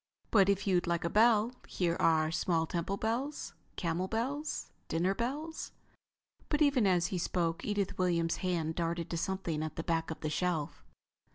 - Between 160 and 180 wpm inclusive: Yes, average, 170 wpm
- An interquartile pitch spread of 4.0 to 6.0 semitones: Yes, average, 4.4 semitones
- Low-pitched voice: No, medium, 180 Hz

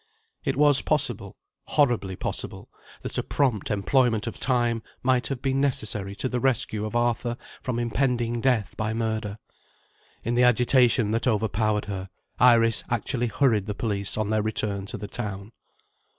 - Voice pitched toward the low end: Yes, low, 115 Hz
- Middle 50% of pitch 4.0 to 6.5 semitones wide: No, average, 2.9 semitones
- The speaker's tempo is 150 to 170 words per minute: Yes, average, 155 wpm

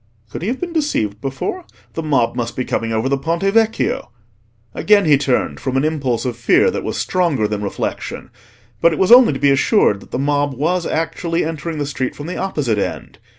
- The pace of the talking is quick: Yes, fast, 210 wpm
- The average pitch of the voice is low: No, medium, 145 Hz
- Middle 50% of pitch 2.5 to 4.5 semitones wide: No, wide, 5.5 semitones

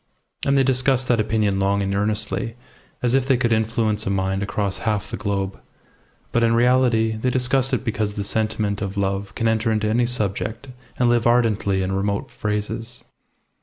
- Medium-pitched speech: No, low, 110 Hz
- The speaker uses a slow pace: No, average, 180 wpm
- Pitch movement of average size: Yes, average, 3.0 semitones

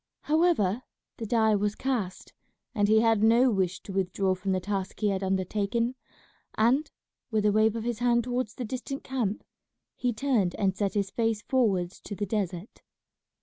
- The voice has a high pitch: Yes, high, 215 Hz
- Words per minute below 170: No, average, 175 wpm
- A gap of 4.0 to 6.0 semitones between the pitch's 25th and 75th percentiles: No, average, 3.5 semitones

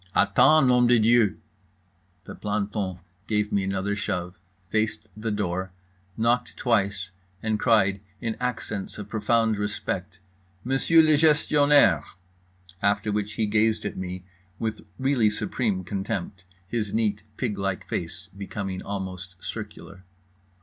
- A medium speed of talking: No, slow, 120 wpm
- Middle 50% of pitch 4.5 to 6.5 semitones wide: No, average, 3.0 semitones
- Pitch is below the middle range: Yes, low, 105 Hz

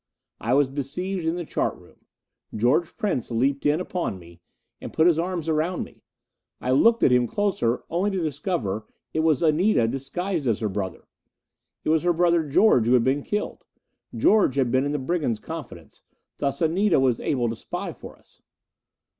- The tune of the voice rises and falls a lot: Yes, wide, 5.8 semitones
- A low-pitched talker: No, medium, 150 Hz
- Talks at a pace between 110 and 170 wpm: No, average, 180 wpm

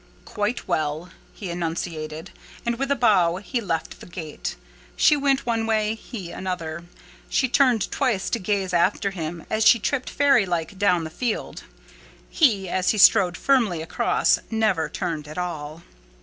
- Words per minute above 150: Yes, average, 160 wpm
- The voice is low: No, high, 190 Hz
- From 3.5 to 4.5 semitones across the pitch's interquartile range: No, average, 5.2 semitones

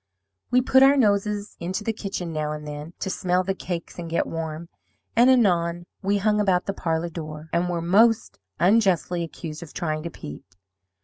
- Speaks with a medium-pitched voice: Yes, medium, 175 Hz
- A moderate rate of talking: Yes, average, 185 wpm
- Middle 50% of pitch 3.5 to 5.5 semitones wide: Yes, average, 3.8 semitones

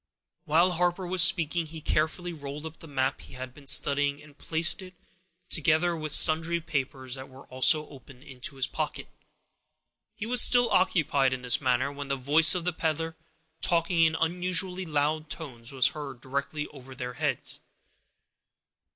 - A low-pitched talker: No, medium, 155 Hz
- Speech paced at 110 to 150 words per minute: No, average, 165 wpm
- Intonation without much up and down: No, average, 3.7 semitones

